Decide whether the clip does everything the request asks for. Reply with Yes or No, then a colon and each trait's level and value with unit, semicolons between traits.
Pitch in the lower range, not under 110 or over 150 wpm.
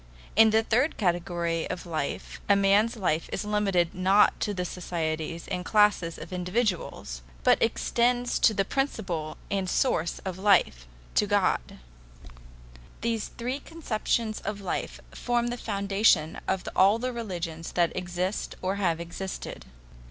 No: high, 195 Hz; slow, 135 wpm